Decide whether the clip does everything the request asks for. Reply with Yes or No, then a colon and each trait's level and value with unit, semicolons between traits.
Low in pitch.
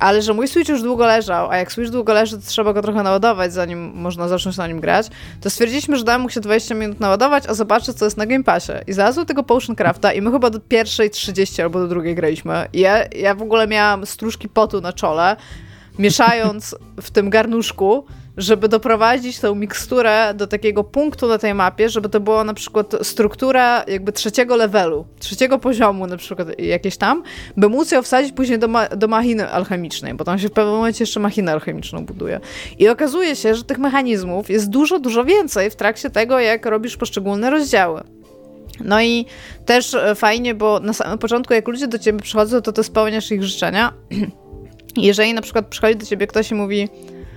No: high, 215 Hz